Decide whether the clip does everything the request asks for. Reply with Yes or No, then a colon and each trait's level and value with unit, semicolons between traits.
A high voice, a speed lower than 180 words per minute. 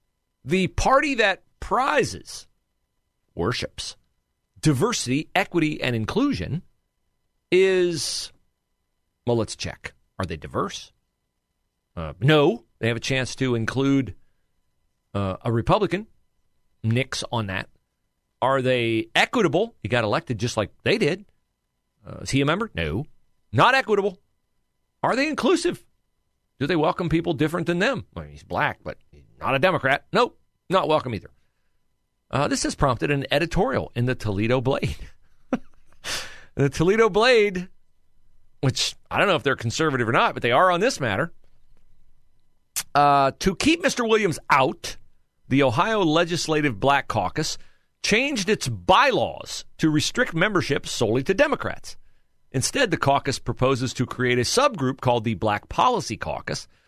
No: low, 130 Hz; average, 140 wpm